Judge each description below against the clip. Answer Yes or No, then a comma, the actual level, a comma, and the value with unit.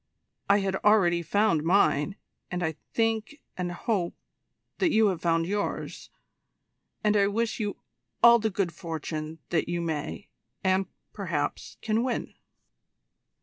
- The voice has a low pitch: No, high, 190 Hz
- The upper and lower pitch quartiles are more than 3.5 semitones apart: Yes, average, 4.1 semitones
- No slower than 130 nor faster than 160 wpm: Yes, slow, 135 wpm